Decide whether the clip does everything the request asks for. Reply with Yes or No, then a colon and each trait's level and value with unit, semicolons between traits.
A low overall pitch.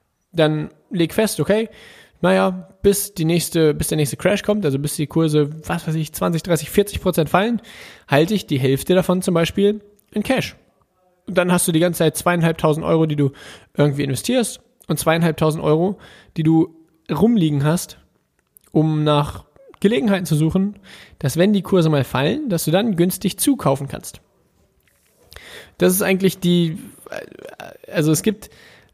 No: medium, 170 Hz